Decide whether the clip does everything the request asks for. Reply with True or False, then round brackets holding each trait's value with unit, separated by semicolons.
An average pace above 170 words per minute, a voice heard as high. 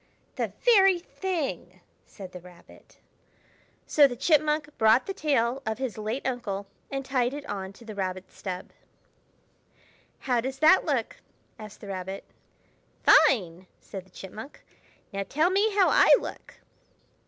False (140 wpm; 245 Hz)